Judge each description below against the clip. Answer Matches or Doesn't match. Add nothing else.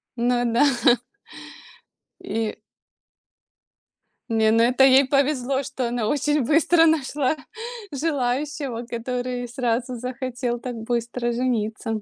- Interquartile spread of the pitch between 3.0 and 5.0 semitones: Doesn't match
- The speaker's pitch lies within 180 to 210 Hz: Doesn't match